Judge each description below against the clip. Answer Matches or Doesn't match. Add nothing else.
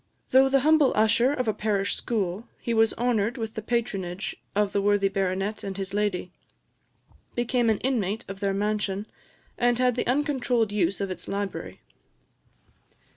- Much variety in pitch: Doesn't match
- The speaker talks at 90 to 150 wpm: Doesn't match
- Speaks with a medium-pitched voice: Doesn't match